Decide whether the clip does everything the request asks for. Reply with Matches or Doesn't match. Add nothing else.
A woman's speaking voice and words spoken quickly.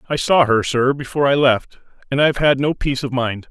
Doesn't match